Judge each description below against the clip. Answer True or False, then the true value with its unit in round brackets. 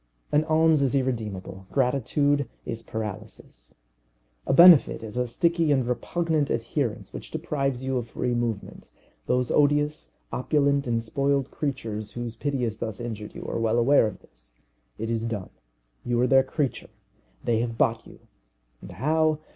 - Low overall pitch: True (125 Hz)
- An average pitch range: True (4.0 semitones)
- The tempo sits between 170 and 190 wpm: False (155 wpm)